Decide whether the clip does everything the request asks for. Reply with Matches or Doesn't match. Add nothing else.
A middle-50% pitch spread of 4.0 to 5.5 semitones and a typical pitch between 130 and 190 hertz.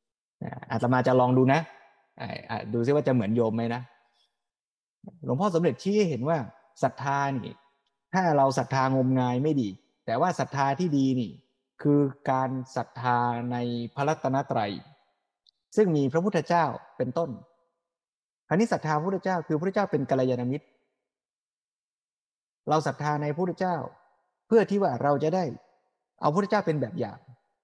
Matches